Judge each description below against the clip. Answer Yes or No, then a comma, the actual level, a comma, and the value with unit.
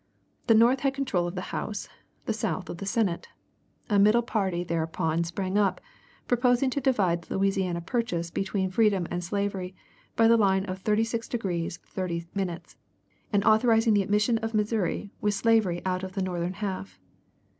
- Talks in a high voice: Yes, high, 195 Hz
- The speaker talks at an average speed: Yes, average, 165 wpm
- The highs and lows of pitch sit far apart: No, average, 3.8 semitones